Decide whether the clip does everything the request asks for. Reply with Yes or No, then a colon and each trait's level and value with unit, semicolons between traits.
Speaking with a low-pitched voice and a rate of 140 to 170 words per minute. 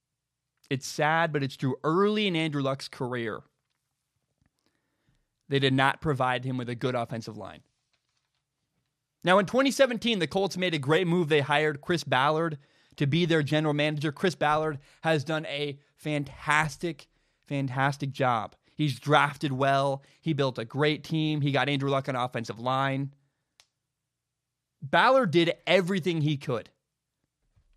No: medium, 145 Hz; average, 145 wpm